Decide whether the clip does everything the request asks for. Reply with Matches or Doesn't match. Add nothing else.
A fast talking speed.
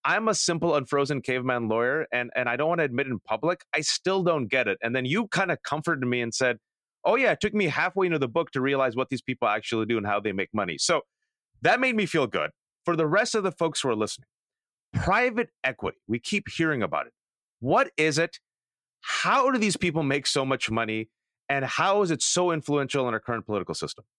Matches